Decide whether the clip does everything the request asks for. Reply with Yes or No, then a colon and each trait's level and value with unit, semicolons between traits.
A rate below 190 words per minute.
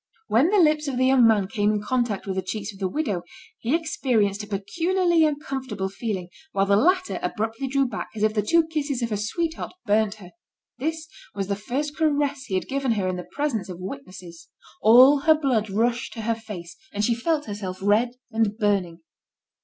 No: average, 200 wpm